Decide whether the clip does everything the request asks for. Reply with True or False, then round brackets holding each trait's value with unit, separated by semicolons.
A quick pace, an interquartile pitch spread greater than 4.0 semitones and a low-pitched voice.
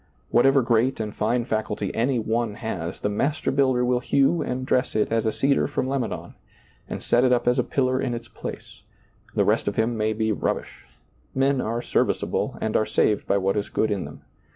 False (210 wpm; 3.0 semitones; 120 Hz)